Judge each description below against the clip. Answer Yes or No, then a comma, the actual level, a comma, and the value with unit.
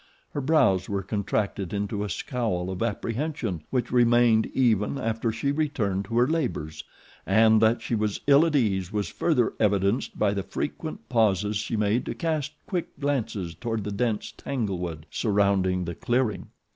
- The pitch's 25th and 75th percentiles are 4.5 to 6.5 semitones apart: No, average, 3.8 semitones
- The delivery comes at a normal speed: Yes, average, 160 wpm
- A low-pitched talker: Yes, low, 110 Hz